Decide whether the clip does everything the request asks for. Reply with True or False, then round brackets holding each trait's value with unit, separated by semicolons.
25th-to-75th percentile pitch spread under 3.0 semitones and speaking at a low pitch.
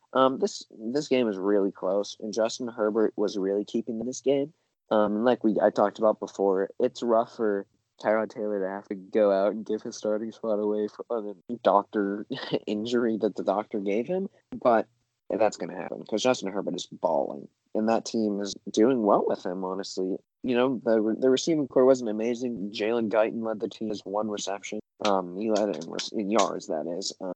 True (2.6 semitones; 110 Hz)